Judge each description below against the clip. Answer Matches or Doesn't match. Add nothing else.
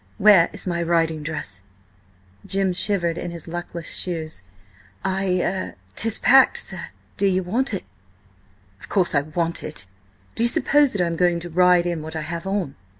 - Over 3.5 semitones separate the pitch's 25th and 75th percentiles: Doesn't match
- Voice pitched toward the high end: Doesn't match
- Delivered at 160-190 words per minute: Matches